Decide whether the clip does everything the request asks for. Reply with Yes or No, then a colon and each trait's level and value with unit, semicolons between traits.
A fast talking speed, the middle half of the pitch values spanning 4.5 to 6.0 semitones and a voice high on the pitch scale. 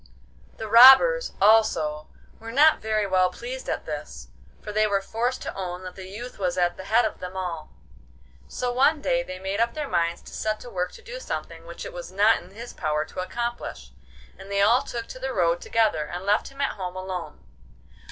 Yes: fast, 210 wpm; average, 4.9 semitones; high, 205 Hz